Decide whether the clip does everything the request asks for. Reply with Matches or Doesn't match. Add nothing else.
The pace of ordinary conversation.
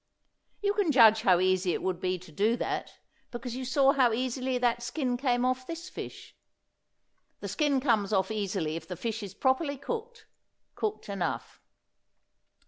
Matches